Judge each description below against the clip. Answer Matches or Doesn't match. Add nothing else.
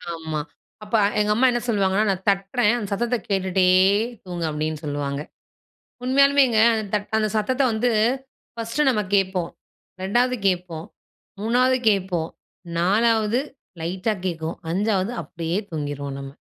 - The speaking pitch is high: Matches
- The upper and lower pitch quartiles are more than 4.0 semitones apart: Matches